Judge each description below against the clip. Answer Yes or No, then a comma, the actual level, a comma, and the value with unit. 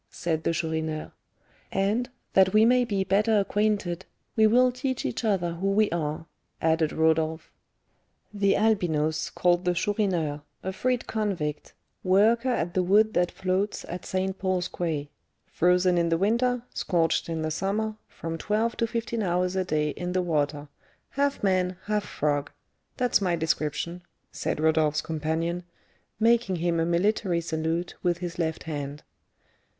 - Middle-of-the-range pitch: Yes, medium, 180 Hz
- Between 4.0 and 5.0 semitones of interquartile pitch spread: Yes, average, 4.4 semitones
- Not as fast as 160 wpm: Yes, average, 150 wpm